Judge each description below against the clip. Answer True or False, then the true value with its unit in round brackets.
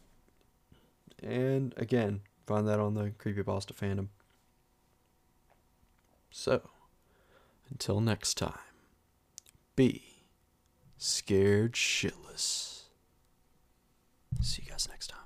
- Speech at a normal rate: False (85 wpm)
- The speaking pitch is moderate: False (105 Hz)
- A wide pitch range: False (3.6 semitones)